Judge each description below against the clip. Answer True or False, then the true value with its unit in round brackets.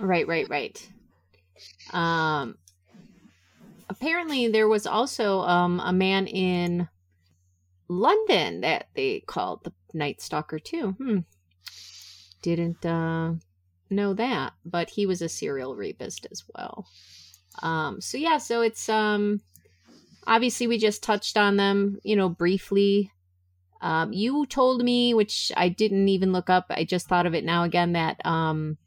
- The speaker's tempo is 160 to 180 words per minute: False (140 wpm)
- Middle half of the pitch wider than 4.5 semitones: True (5.6 semitones)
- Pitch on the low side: False (180 Hz)